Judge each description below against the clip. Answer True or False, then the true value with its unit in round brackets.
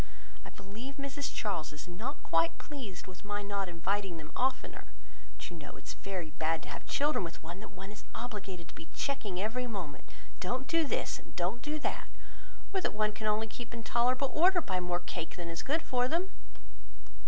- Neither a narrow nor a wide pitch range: False (6.4 semitones)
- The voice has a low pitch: False (205 Hz)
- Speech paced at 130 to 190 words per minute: False (205 wpm)